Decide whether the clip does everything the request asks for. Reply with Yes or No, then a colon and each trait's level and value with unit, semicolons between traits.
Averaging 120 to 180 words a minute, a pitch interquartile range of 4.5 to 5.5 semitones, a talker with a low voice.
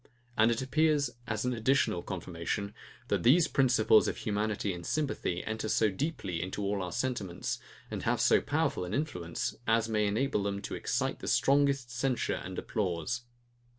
Yes: average, 165 wpm; average, 5.1 semitones; low, 110 Hz